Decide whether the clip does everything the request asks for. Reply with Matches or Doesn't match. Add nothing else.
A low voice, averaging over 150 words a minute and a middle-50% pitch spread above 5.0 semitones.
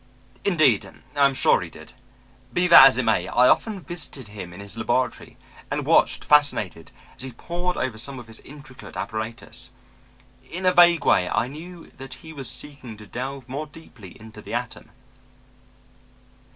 Matches